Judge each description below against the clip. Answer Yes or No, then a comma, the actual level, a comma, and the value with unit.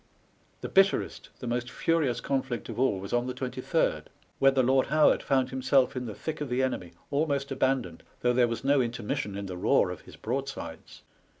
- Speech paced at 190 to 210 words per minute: Yes, average, 200 wpm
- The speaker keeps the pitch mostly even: Yes, narrow, 2.2 semitones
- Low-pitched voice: Yes, low, 130 Hz